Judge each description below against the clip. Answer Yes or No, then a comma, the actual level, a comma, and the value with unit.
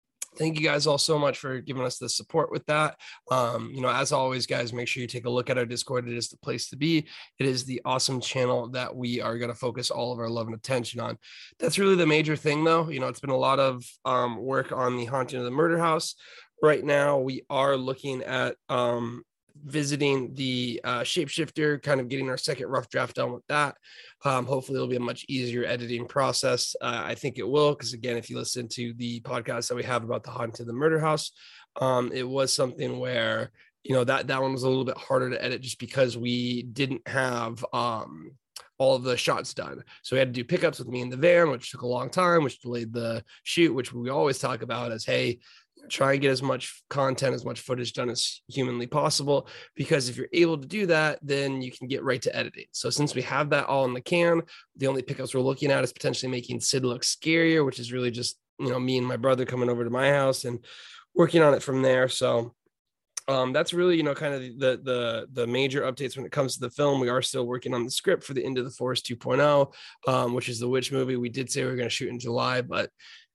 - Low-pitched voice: Yes, low, 130 Hz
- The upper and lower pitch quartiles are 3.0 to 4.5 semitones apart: No, narrow, 2.5 semitones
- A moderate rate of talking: No, fast, 245 wpm